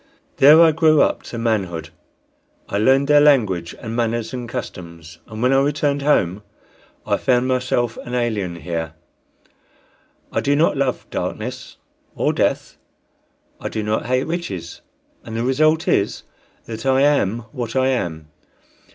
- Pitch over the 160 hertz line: No, low, 120 Hz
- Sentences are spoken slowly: No, average, 150 wpm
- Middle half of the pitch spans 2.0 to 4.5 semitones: No, wide, 5.4 semitones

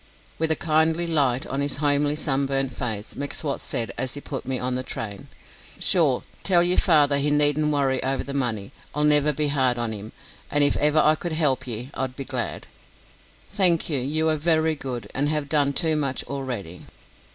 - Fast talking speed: No, average, 195 wpm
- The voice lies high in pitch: No, medium, 140 Hz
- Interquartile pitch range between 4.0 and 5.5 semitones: No, average, 2.8 semitones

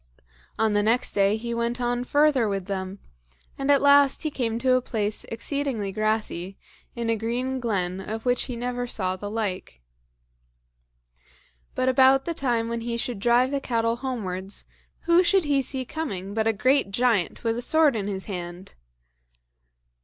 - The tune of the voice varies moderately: Yes, average, 4.0 semitones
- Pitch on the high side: Yes, high, 235 Hz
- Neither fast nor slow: Yes, average, 170 wpm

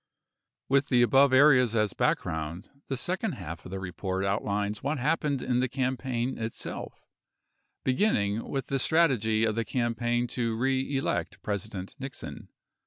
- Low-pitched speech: Yes, low, 120 Hz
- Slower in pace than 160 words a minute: Yes, average, 140 wpm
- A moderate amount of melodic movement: Yes, average, 4.5 semitones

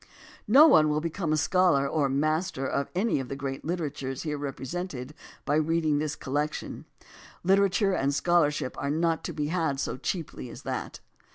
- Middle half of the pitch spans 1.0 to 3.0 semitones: No, average, 3.7 semitones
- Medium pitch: Yes, medium, 155 Hz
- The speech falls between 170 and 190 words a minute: Yes, average, 175 wpm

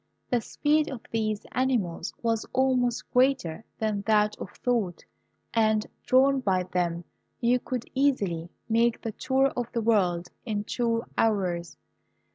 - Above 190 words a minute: No, slow, 135 wpm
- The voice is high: Yes, high, 225 Hz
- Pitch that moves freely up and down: No, average, 4.0 semitones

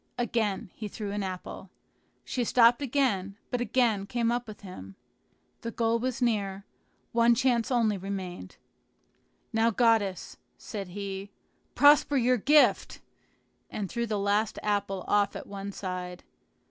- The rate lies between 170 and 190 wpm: No, slow, 135 wpm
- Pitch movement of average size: Yes, average, 3.3 semitones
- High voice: Yes, high, 210 Hz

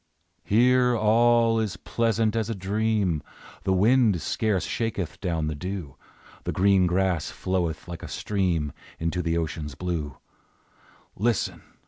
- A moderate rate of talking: No, slow, 130 wpm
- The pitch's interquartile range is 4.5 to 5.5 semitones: Yes, average, 4.8 semitones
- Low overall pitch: Yes, very low, 95 Hz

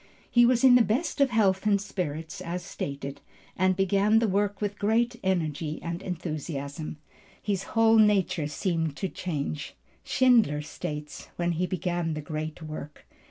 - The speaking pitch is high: No, medium, 180 Hz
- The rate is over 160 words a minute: No, average, 155 wpm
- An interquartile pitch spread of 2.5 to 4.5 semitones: No, average, 5.1 semitones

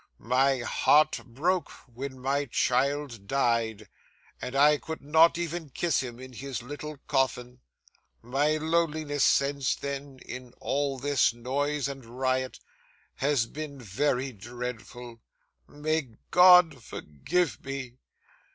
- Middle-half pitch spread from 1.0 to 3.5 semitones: Yes, average, 3.0 semitones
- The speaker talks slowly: Yes, slow, 115 wpm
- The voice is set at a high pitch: No, low, 135 Hz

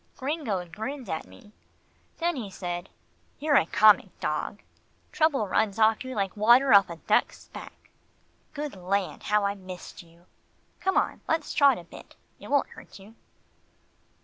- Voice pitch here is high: Yes, high, 210 Hz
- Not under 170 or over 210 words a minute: No, average, 155 wpm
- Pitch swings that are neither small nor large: No, wide, 6.8 semitones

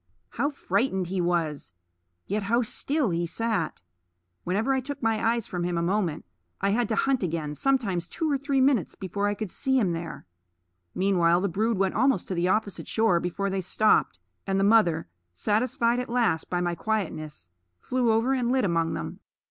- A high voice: Yes, high, 200 Hz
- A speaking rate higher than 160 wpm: Yes, average, 190 wpm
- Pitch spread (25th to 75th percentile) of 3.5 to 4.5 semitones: No, average, 5.3 semitones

